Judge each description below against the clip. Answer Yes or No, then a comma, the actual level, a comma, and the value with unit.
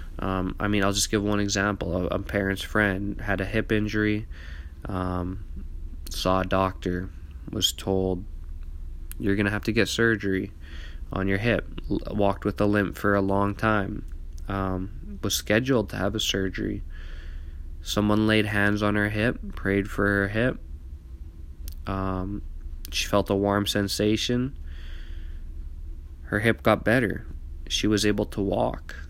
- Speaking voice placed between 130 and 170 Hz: No, very low, 95 Hz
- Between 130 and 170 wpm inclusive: Yes, average, 150 wpm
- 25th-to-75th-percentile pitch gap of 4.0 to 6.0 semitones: Yes, wide, 5.6 semitones